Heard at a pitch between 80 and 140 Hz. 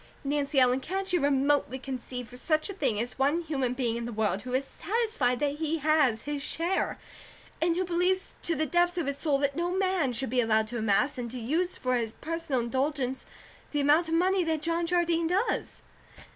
No: very high, 290 Hz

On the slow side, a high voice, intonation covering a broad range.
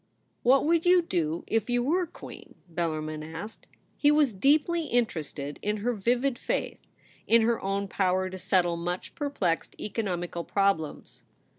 No: average, 155 wpm; high, 200 Hz; wide, 6.5 semitones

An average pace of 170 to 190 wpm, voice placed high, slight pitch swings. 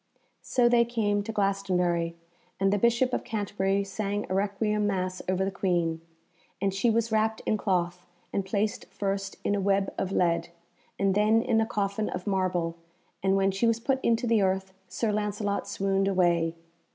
Yes: average, 175 wpm; high, 195 Hz; narrow, 2.1 semitones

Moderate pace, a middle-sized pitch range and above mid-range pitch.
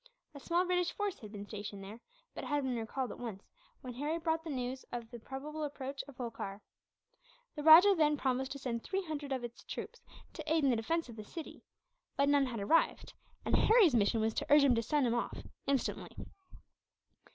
No: fast, 210 wpm; average, 4.9 semitones; very high, 270 Hz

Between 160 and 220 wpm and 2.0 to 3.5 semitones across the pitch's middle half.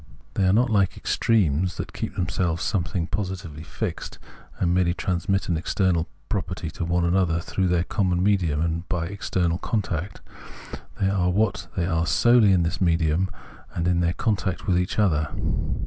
Yes: average, 175 wpm; narrow, 2.4 semitones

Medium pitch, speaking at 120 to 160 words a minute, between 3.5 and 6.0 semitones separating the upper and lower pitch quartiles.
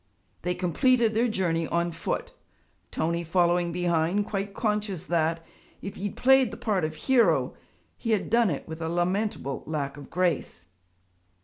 Yes: medium, 175 Hz; average, 155 wpm; average, 4.2 semitones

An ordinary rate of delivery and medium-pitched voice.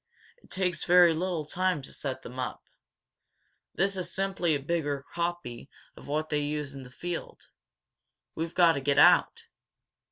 Yes: average, 160 wpm; medium, 160 Hz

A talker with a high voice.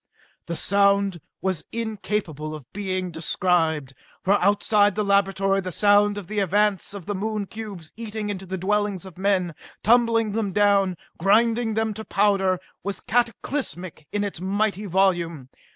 Yes: high, 200 Hz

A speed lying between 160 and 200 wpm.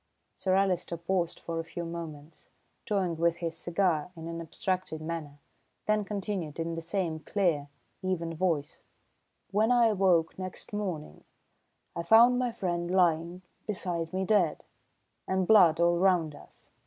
No: average, 145 wpm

